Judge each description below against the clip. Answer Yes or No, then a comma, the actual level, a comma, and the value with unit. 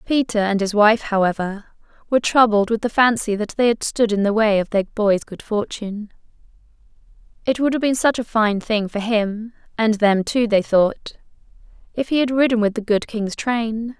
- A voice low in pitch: No, high, 220 Hz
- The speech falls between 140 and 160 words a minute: No, average, 195 wpm